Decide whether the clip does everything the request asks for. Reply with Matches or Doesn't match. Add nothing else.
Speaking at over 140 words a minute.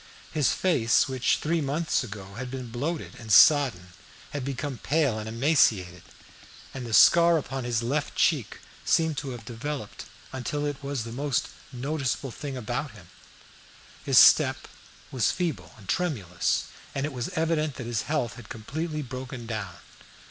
Matches